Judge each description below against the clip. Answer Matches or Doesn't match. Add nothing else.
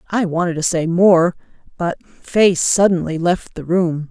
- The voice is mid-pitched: Matches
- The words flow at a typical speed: Matches